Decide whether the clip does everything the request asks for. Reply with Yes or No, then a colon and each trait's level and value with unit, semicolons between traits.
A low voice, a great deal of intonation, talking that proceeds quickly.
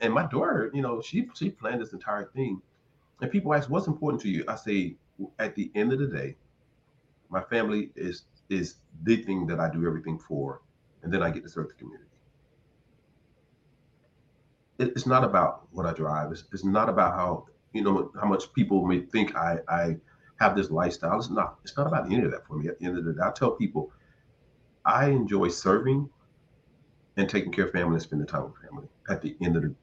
Yes: low, 115 Hz; wide, 8.0 semitones; fast, 215 wpm